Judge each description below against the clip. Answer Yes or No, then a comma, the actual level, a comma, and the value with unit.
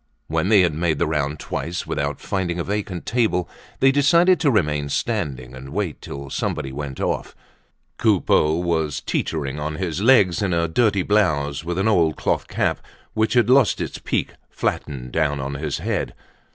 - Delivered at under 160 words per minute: No, average, 175 wpm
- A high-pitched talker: No, very low, 85 Hz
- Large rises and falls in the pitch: Yes, wide, 5.9 semitones